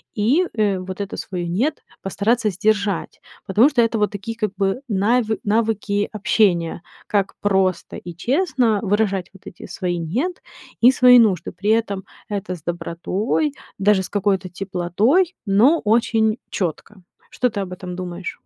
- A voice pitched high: Yes, high, 205 Hz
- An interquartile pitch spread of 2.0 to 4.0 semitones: Yes, average, 3.4 semitones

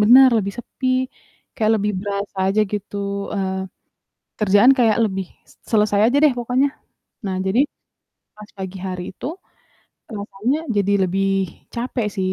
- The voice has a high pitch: Yes, high, 205 Hz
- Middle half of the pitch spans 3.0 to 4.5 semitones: Yes, average, 3.4 semitones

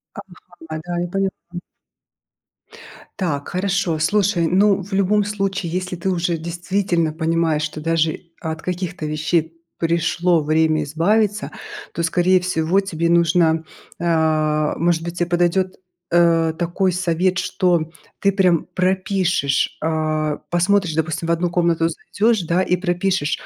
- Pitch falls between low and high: Yes, medium, 175 Hz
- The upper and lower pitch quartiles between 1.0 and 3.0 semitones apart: Yes, narrow, 2.5 semitones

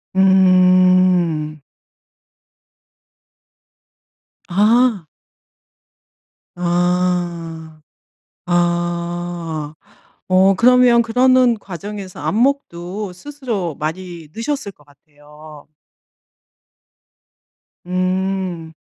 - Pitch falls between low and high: Yes, medium, 180 Hz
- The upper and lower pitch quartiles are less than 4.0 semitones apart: Yes, average, 3.1 semitones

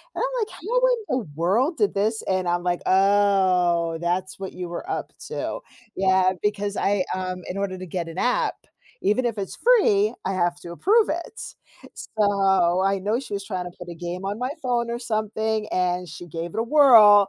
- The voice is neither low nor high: No, high, 195 Hz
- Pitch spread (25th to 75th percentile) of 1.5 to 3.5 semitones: No, average, 4.0 semitones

